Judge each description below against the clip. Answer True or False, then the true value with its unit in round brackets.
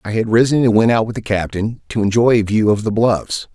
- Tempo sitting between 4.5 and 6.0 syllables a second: True (5.7 syllables/s)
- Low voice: True (110 Hz)